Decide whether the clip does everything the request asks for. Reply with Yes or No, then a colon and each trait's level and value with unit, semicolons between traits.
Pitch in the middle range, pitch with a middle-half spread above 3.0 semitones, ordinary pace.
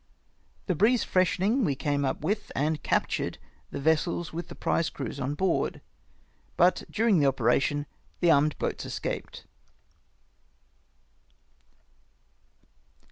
No: medium, 160 Hz; average, 4.4 semitones; slow, 115 wpm